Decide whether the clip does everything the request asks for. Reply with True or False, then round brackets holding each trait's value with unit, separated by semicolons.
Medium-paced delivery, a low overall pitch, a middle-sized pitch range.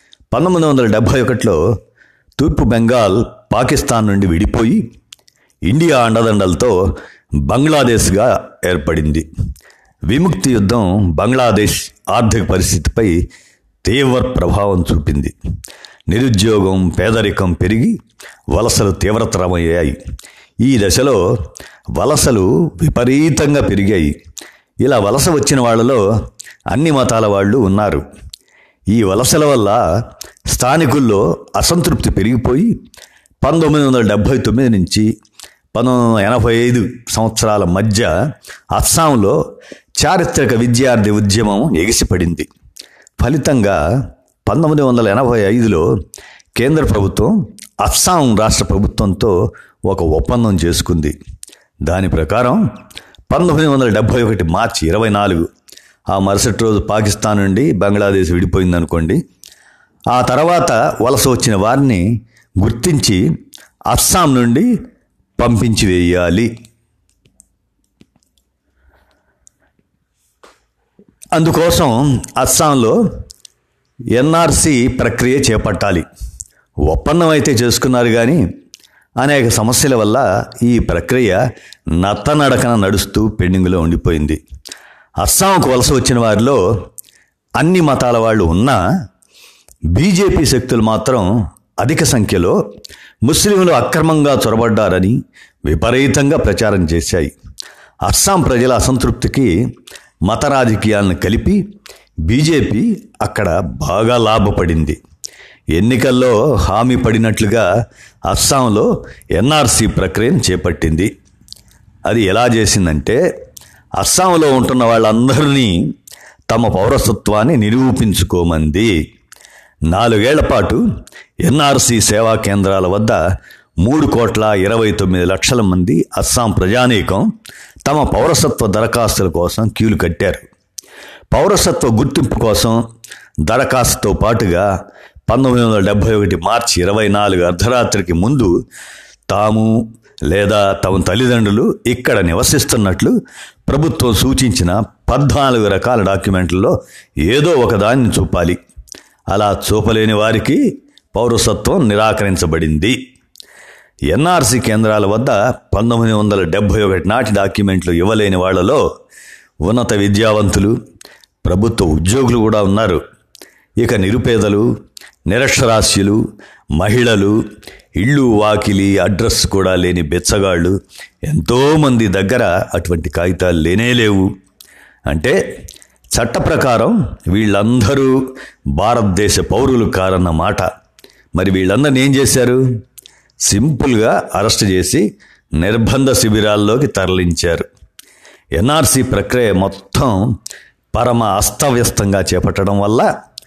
True (85 wpm; 110 Hz; 4.6 semitones)